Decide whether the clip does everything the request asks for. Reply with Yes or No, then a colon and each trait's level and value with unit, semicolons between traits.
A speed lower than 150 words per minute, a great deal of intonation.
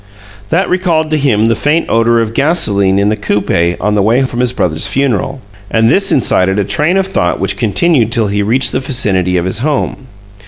No: fast, 205 wpm; wide, 5.7 semitones